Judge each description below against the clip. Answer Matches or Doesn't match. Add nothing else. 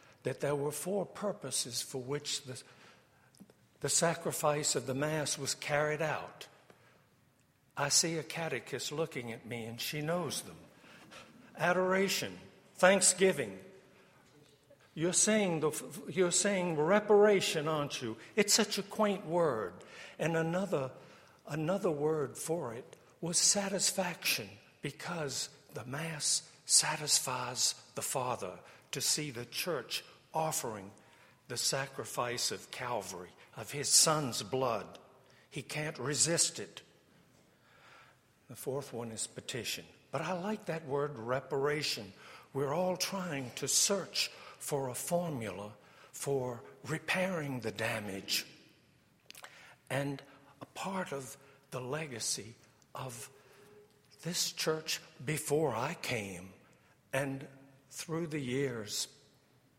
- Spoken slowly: Matches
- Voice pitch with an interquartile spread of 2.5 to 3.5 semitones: Doesn't match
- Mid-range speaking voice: Matches